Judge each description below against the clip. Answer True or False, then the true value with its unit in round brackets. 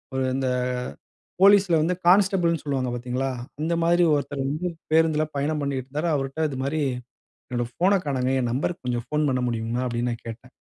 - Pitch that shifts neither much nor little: True (4.5 semitones)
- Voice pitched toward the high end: False (140 Hz)